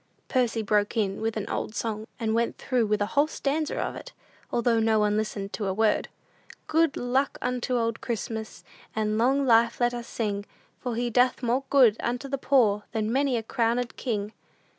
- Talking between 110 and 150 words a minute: No, average, 190 wpm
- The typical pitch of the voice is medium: No, high, 230 Hz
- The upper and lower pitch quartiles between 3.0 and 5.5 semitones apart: No, narrow, 2.5 semitones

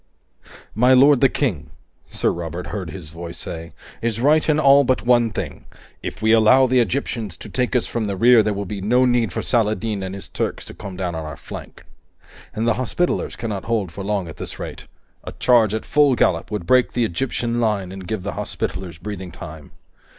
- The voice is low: Yes, low, 110 Hz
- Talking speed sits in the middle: No, fast, 210 wpm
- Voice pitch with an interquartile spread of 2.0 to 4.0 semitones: No, average, 4.7 semitones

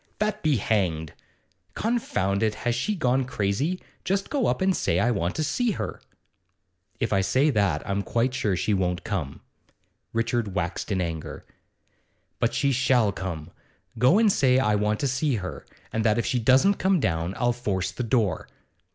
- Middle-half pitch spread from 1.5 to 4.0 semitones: No, wide, 5.6 semitones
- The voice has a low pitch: Yes, low, 115 Hz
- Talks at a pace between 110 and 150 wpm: No, average, 175 wpm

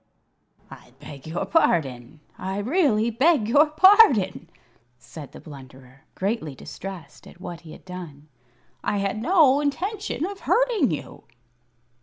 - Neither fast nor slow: No, slow, 130 wpm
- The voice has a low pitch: No, high, 200 Hz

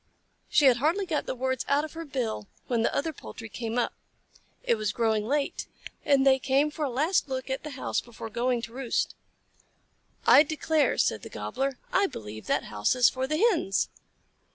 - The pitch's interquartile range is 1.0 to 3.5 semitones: No, average, 4.3 semitones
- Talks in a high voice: Yes, very high, 265 Hz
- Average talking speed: Yes, average, 195 wpm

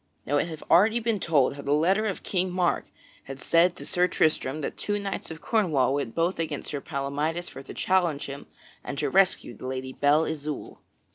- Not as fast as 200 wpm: No, fast, 205 wpm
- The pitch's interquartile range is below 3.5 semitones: No, average, 4.3 semitones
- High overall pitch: No, medium, 160 Hz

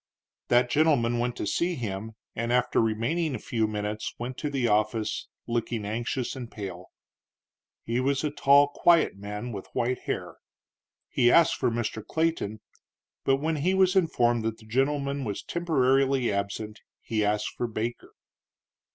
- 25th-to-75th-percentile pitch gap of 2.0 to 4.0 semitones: No, average, 4.4 semitones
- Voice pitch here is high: No, low, 120 Hz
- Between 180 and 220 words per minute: No, average, 155 wpm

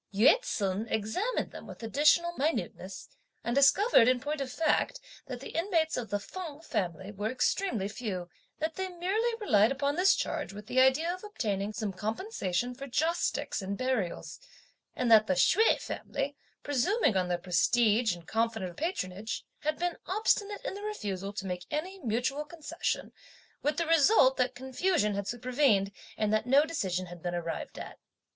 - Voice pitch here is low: No, very high, 255 Hz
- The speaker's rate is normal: Yes, average, 170 wpm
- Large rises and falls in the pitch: Yes, wide, 8.1 semitones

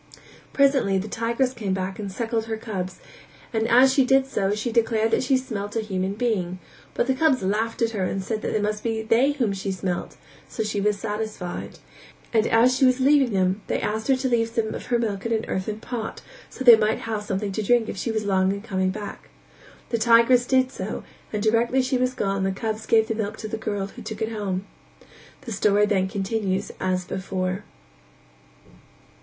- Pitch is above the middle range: Yes, high, 220 Hz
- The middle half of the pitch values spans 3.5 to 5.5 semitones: No, average, 3.1 semitones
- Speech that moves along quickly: Yes, fast, 210 wpm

